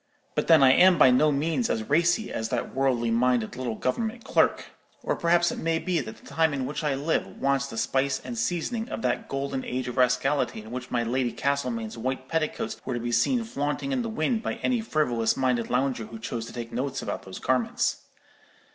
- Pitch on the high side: No, low, 135 Hz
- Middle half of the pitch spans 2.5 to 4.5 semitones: No, average, 5.0 semitones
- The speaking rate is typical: No, fast, 215 wpm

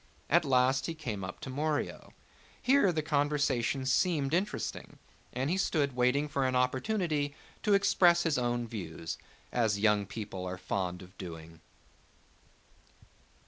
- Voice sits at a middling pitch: No, low, 130 Hz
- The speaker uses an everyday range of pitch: No, wide, 6.5 semitones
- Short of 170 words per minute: Yes, average, 140 wpm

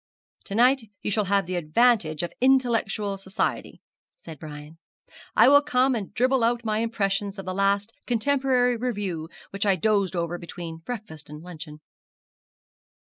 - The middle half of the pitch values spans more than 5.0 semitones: Yes, wide, 5.5 semitones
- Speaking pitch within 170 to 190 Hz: No, high, 200 Hz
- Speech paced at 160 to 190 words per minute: No, average, 150 wpm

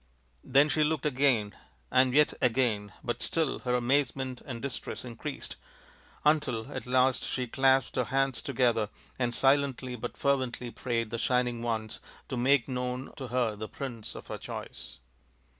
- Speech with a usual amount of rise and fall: No, narrow, 2.3 semitones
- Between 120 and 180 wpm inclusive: Yes, average, 160 wpm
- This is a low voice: Yes, low, 125 Hz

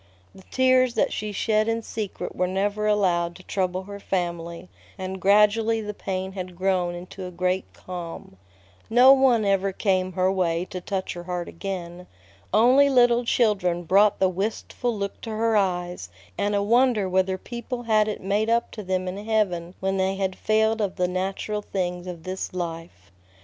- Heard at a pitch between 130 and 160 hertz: No, high, 195 Hz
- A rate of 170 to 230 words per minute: Yes, average, 175 wpm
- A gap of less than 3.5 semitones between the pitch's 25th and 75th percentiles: Yes, average, 2.9 semitones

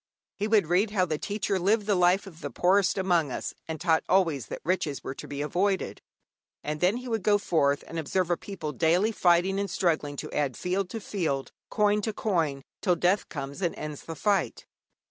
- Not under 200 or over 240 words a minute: Yes, fast, 205 wpm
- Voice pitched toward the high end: No, medium, 180 Hz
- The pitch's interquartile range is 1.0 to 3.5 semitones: No, average, 4.3 semitones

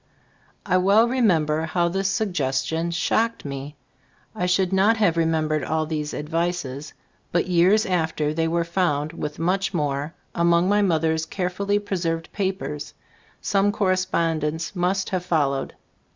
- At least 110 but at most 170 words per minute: Yes, average, 140 wpm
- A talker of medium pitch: Yes, medium, 170 Hz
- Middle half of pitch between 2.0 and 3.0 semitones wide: No, average, 3.4 semitones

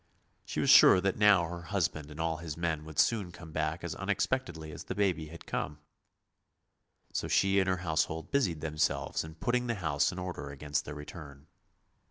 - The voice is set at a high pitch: No, very low, 85 Hz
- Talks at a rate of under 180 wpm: No, average, 190 wpm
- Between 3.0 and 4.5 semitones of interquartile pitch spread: Yes, average, 3.5 semitones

